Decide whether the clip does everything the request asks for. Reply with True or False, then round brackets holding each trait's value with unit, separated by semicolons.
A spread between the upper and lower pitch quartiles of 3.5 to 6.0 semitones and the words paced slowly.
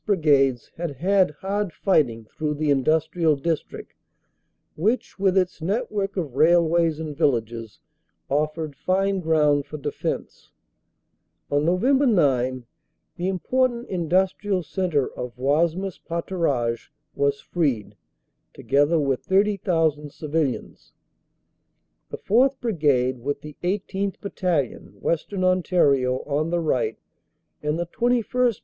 True (5.0 semitones; 115 wpm)